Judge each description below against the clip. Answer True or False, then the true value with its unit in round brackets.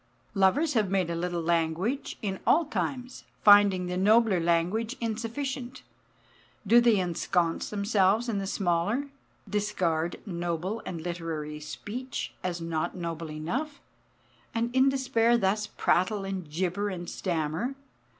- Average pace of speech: False (130 wpm)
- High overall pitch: True (195 Hz)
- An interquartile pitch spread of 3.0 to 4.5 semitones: False (5.2 semitones)